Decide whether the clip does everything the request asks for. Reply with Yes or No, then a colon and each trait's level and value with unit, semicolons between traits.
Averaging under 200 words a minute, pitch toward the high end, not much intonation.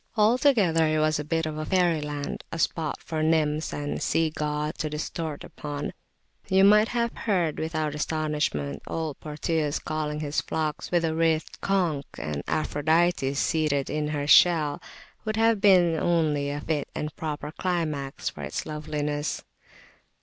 No: average, 150 wpm; medium, 155 Hz; narrow, 2.0 semitones